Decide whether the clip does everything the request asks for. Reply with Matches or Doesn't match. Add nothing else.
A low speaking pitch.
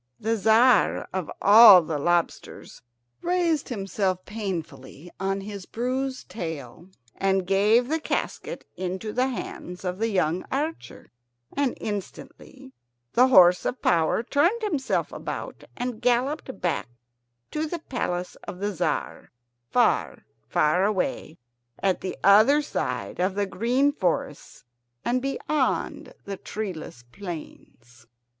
Doesn't match